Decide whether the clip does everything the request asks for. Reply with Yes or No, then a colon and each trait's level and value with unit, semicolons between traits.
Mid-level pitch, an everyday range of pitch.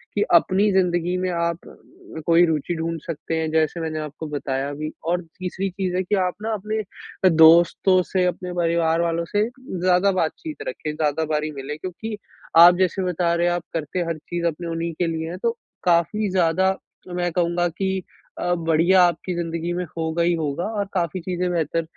No: medium, 170 Hz; narrow, 2.1 semitones